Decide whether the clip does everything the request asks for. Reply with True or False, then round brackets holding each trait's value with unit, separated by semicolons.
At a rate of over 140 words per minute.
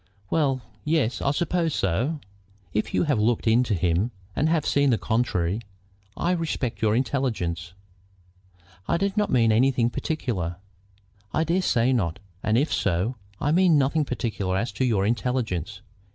True (155 wpm)